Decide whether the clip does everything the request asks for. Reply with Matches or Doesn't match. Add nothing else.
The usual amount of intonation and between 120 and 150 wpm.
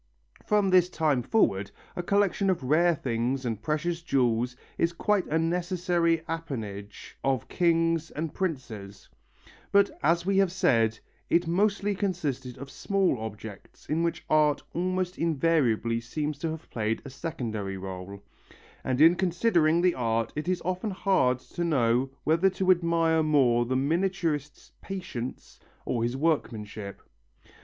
Doesn't match